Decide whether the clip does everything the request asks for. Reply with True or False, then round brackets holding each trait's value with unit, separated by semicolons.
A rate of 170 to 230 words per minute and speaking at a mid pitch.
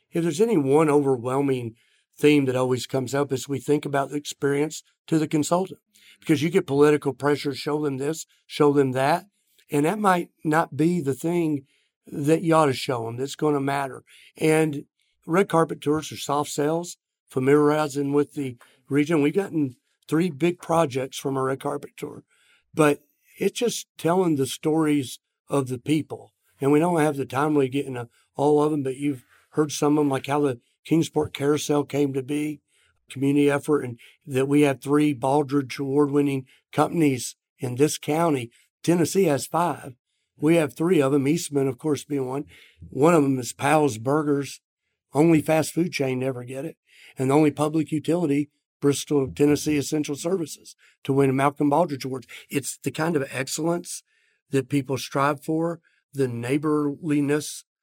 True (175 wpm; 145 Hz)